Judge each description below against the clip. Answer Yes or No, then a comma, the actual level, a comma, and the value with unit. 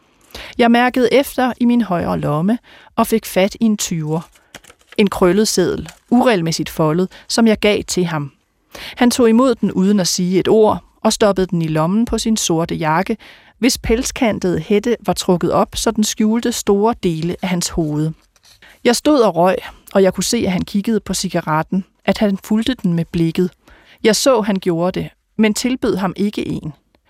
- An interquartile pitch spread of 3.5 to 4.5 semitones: Yes, average, 4.2 semitones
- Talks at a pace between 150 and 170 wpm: No, average, 190 wpm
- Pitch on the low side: No, high, 205 Hz